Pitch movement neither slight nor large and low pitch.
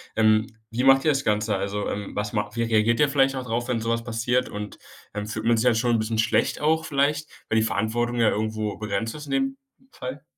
Yes: average, 3.2 semitones; low, 115 Hz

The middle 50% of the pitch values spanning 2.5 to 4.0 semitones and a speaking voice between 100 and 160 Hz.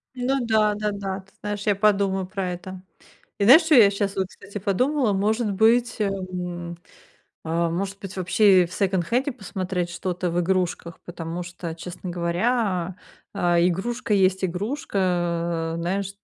No: average, 2.8 semitones; high, 190 Hz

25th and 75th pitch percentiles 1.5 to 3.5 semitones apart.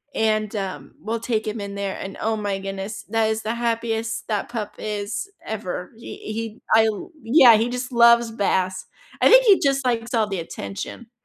Yes: narrow, 2.6 semitones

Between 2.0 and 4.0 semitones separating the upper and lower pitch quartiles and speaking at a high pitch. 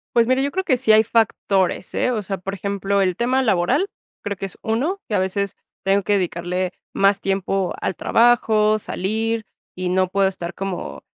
Yes: average, 3.2 semitones; high, 200 Hz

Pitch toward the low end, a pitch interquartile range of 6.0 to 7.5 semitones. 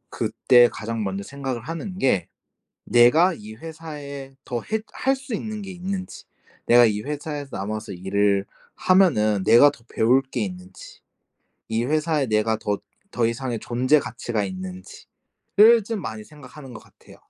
Yes: low, 125 Hz; wide, 6.4 semitones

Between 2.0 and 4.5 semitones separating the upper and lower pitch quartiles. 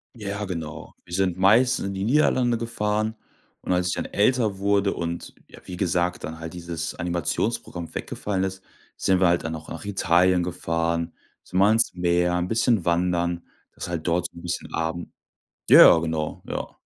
Yes: average, 2.9 semitones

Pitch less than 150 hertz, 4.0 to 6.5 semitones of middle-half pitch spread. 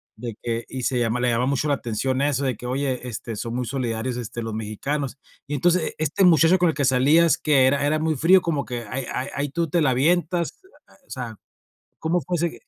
Yes: low, 135 Hz; average, 4.4 semitones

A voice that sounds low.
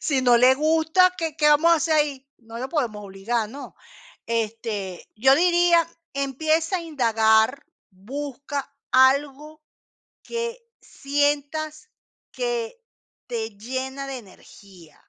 No: very high, 275 Hz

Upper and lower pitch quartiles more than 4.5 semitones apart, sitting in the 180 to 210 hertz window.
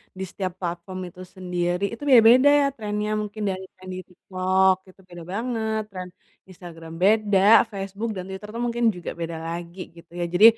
No: average, 3.3 semitones; high, 190 Hz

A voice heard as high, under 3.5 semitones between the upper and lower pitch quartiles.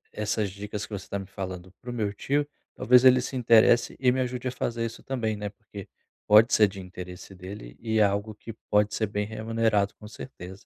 No: low, 105 Hz; average, 2.7 semitones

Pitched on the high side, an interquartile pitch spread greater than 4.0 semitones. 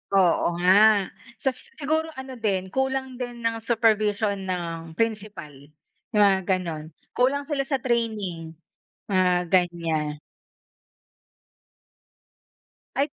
Yes: high, 210 Hz; wide, 5.6 semitones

